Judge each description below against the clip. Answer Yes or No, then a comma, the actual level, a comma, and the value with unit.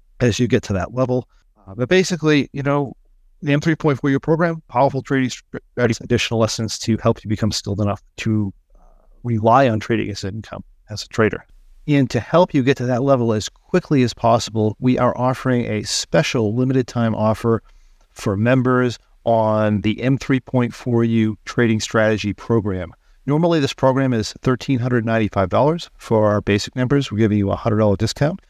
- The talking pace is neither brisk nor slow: Yes, average, 160 wpm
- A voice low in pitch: Yes, low, 120 Hz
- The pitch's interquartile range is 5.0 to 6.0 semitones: No, average, 3.9 semitones